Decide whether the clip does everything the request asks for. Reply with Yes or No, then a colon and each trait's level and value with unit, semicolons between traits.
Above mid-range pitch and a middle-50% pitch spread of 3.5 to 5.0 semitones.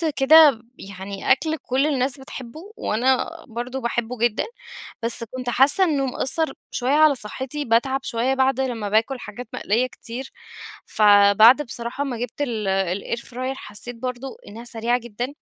No: high, 245 Hz; average, 2.8 semitones